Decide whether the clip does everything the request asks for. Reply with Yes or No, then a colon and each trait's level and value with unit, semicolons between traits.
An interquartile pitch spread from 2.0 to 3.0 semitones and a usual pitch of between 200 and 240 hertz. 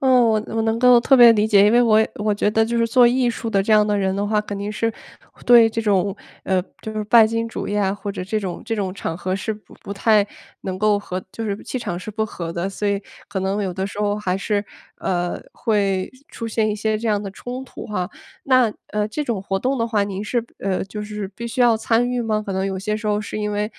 Yes: narrow, 2.4 semitones; high, 210 Hz